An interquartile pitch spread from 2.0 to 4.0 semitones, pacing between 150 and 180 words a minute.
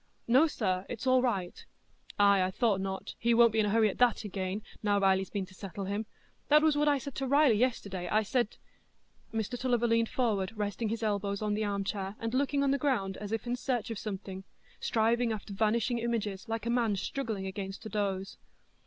No: average, 3.3 semitones; fast, 205 wpm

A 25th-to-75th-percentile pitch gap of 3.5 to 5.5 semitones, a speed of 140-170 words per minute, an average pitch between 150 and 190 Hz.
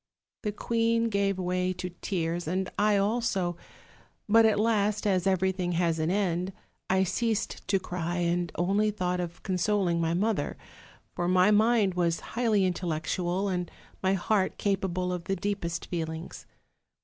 No: average, 2.8 semitones; average, 150 wpm; medium, 185 Hz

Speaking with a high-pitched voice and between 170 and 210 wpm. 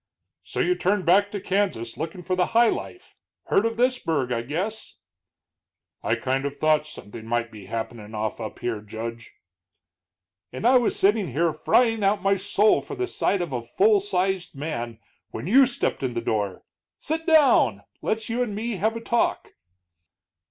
No: medium, 180 Hz; average, 175 wpm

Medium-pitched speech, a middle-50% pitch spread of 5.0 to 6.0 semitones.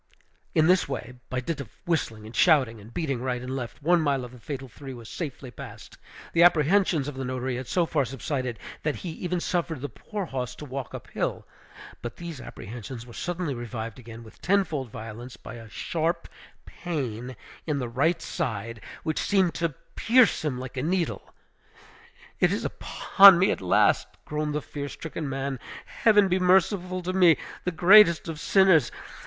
Yes: medium, 145 Hz; wide, 5.6 semitones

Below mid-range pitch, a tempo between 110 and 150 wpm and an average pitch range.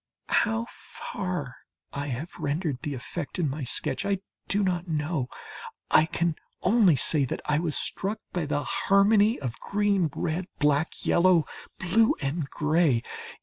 No: medium, 165 Hz; average, 145 wpm; average, 4.7 semitones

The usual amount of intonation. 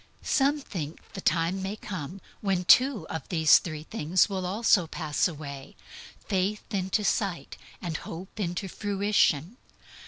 Yes: average, 3.8 semitones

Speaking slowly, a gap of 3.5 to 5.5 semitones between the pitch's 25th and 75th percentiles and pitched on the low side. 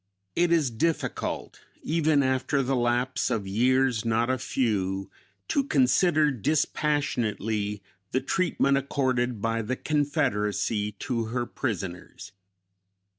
Yes: slow, 110 wpm; average, 4.5 semitones; low, 125 Hz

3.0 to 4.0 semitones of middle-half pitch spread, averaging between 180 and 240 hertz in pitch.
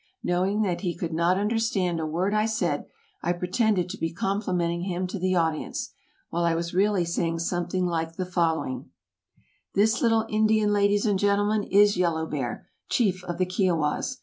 Yes: average, 3.3 semitones; medium, 185 Hz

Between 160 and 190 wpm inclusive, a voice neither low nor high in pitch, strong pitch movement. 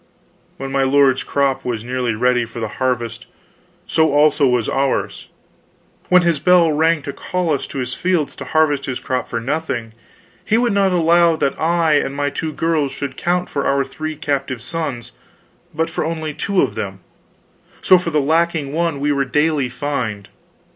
No: average, 180 wpm; medium, 145 Hz; average, 3.9 semitones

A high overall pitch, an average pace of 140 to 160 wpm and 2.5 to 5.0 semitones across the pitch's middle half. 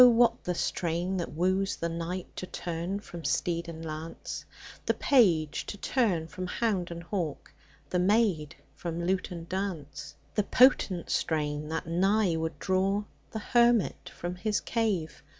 No: medium, 180 Hz; average, 150 wpm; average, 3.4 semitones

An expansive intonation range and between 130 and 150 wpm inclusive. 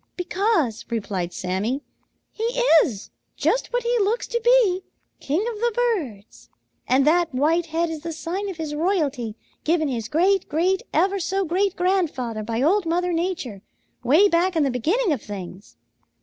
No: wide, 7.2 semitones; average, 165 wpm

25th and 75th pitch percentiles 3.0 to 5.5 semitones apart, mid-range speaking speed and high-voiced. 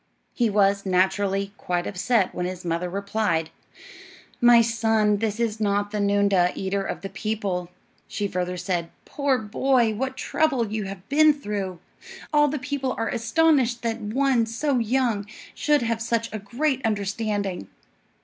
Yes: average, 3.5 semitones; average, 150 wpm; high, 215 Hz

